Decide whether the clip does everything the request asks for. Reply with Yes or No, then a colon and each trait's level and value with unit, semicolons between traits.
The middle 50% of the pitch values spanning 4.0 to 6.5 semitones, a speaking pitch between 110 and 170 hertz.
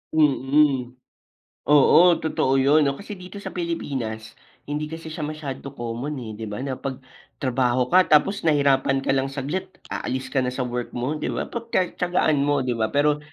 No: average, 3.2 semitones; medium, 140 Hz